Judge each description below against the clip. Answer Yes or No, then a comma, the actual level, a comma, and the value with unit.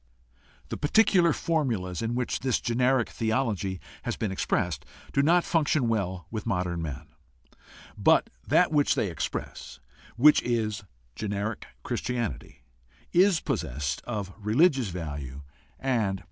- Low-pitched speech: Yes, low, 110 Hz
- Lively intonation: Yes, wide, 6.5 semitones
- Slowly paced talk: Yes, slow, 130 wpm